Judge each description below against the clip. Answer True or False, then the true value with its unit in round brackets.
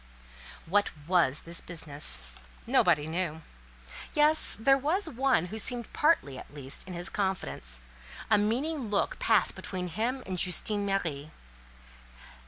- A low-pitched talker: False (190 Hz)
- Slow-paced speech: True (130 wpm)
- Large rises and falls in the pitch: True (6.5 semitones)